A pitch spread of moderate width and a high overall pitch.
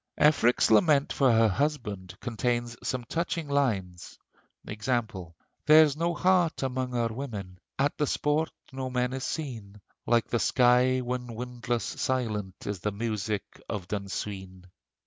No: average, 4.7 semitones; low, 120 Hz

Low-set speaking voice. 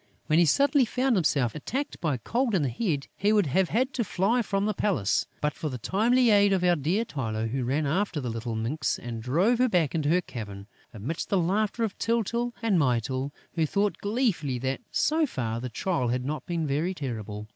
No: medium, 165 Hz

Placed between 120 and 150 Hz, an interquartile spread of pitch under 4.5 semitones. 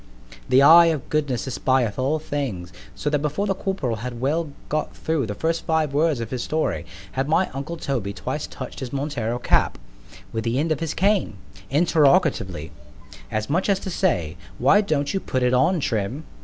No: medium, 140 Hz; average, 5.1 semitones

